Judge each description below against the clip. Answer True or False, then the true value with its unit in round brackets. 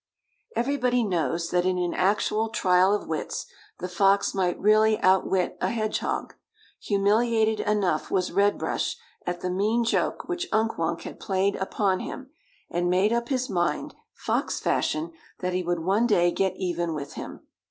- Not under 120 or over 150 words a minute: False (165 wpm)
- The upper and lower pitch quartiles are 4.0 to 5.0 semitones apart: False (3.5 semitones)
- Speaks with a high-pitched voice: True (195 Hz)